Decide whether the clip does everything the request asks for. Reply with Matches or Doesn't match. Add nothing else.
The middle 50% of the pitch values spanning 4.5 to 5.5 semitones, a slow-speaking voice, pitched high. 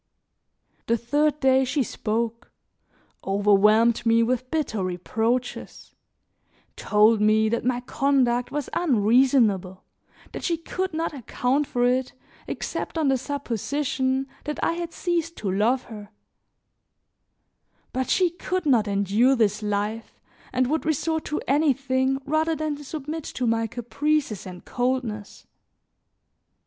Matches